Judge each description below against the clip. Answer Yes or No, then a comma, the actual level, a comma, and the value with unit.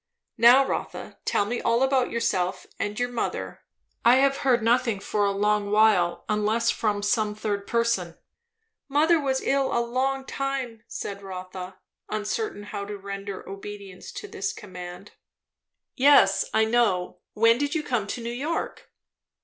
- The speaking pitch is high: Yes, high, 220 Hz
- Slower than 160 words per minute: Yes, average, 150 wpm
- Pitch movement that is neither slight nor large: Yes, average, 3.9 semitones